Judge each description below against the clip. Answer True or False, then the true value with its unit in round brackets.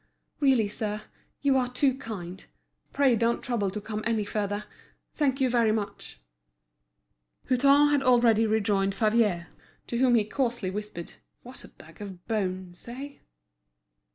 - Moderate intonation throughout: True (3.7 semitones)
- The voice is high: True (225 Hz)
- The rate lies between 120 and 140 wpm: True (135 wpm)